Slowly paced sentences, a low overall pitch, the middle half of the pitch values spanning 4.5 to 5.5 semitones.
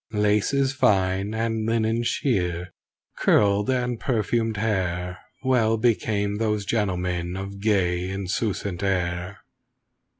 No: slow, 100 wpm; low, 105 Hz; average, 3.3 semitones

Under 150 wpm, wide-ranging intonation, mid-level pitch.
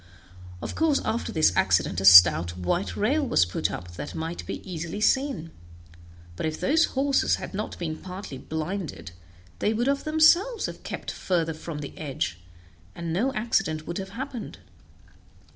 No: average, 160 wpm; wide, 8.5 semitones; medium, 180 Hz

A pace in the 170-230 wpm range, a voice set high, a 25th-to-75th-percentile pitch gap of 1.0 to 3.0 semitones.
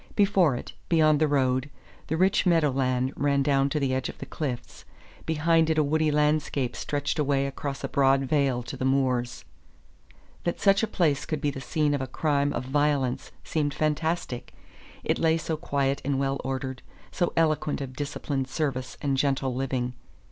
No: average, 180 wpm; medium, 140 Hz; narrow, 2.6 semitones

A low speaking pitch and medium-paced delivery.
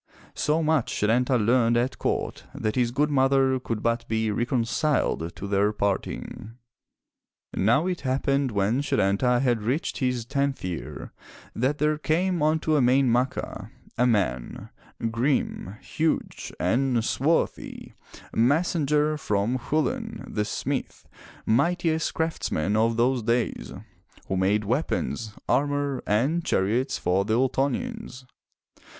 No: low, 125 Hz; slow, 120 wpm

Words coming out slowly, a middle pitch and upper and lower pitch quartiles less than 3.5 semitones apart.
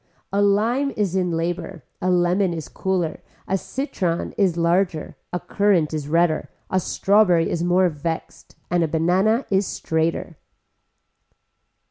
Yes: slow, 130 wpm; medium, 180 Hz; average, 2.8 semitones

